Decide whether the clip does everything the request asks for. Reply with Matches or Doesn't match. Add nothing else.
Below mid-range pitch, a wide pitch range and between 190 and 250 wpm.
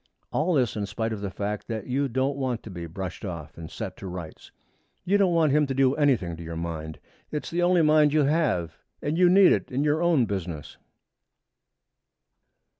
Matches